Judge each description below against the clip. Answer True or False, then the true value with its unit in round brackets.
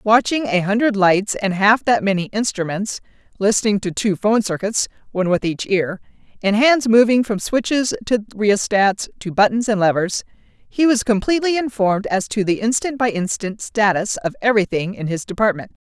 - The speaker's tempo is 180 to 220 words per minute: False (170 wpm)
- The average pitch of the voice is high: True (210 Hz)